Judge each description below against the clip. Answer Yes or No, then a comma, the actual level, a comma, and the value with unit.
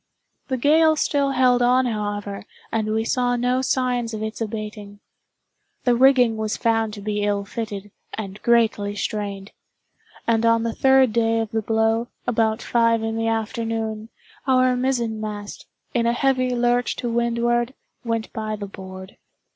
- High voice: Yes, high, 225 Hz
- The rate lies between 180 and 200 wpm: No, average, 155 wpm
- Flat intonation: Yes, narrow, 2.3 semitones